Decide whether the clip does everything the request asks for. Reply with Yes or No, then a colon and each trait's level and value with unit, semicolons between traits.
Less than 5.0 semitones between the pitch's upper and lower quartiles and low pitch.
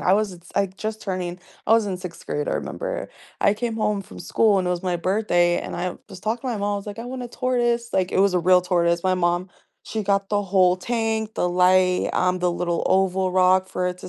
No: average, 3.0 semitones; high, 190 Hz